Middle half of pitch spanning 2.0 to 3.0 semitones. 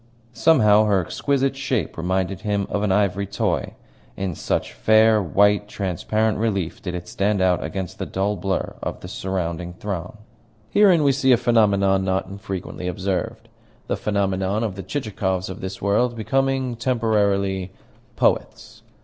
Yes: average, 2.7 semitones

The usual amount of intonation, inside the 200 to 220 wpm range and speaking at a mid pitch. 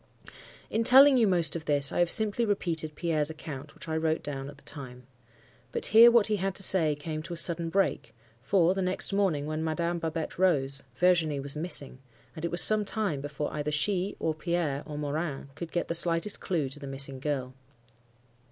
Yes: average, 3.9 semitones; fast, 205 wpm; medium, 160 Hz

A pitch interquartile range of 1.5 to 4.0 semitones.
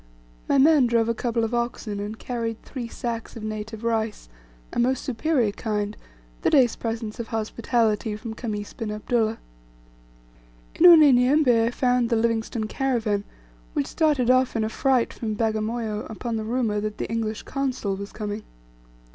Yes: narrow, 2.4 semitones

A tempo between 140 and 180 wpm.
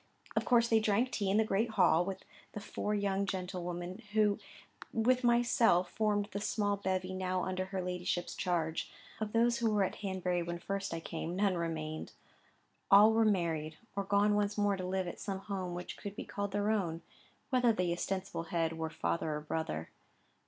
No: average, 190 wpm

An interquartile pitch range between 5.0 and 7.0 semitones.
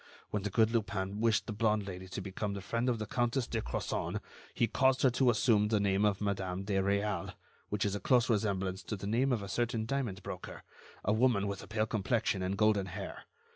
No: average, 2.8 semitones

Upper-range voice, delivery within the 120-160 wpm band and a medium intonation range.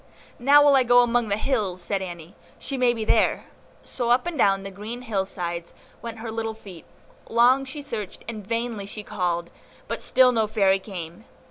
No: high, 220 Hz; average, 195 wpm; average, 3.9 semitones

